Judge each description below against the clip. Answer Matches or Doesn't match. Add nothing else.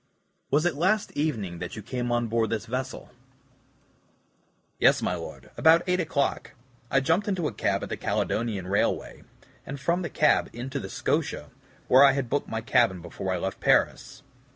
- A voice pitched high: Doesn't match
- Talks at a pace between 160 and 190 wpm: Matches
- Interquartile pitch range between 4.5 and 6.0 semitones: Matches